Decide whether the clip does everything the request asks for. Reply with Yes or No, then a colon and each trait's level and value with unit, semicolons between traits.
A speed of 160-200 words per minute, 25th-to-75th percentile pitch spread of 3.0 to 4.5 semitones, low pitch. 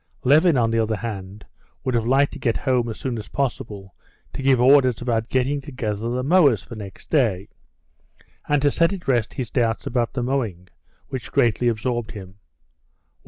Yes: average, 180 wpm; average, 3.5 semitones; low, 120 Hz